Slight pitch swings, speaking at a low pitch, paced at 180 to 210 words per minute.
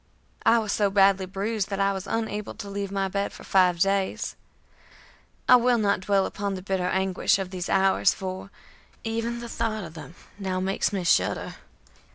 No: narrow, 1.7 semitones; high, 195 Hz; average, 185 wpm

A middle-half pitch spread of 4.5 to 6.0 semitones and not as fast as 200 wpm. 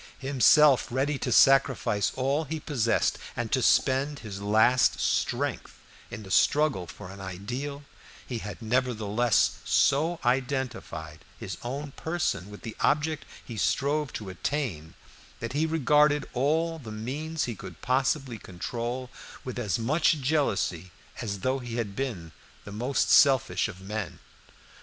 Yes: average, 5.1 semitones; average, 140 wpm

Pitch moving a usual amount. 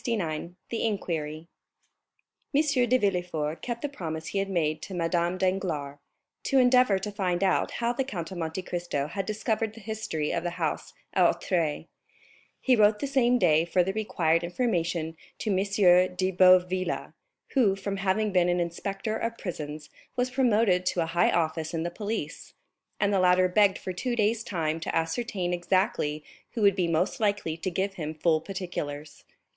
Yes: average, 4.3 semitones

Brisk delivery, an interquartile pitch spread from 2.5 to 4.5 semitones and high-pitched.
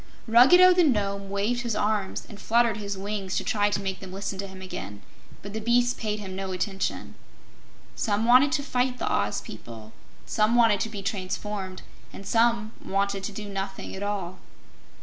No: average, 180 wpm; average, 2.9 semitones; high, 205 Hz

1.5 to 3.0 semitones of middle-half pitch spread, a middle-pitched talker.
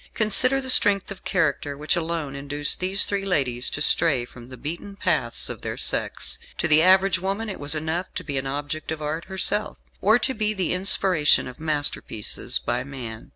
No: average, 5.3 semitones; medium, 160 Hz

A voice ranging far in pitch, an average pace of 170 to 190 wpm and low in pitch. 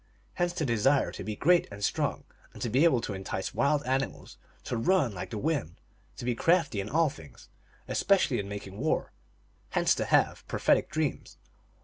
Yes: wide, 7.4 semitones; average, 185 wpm; low, 130 Hz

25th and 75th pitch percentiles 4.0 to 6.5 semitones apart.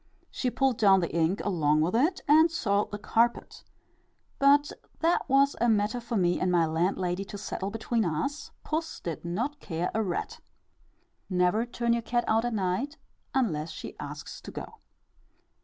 Yes: wide, 5.6 semitones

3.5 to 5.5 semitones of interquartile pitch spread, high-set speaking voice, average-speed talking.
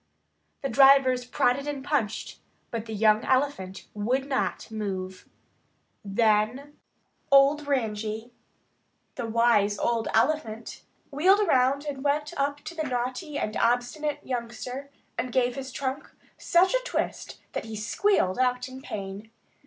No: average, 4.2 semitones; very high, 250 Hz; slow, 130 wpm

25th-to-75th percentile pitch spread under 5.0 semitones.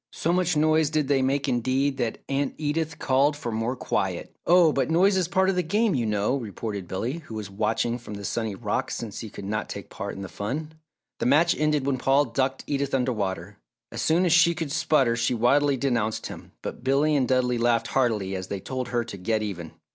No: average, 5.3 semitones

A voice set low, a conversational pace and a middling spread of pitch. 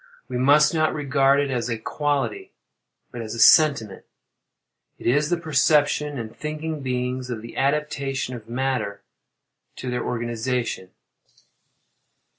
No: low, 130 Hz; slow, 125 wpm; average, 3.9 semitones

